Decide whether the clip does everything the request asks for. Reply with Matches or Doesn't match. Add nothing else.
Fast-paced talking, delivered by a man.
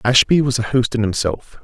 Matches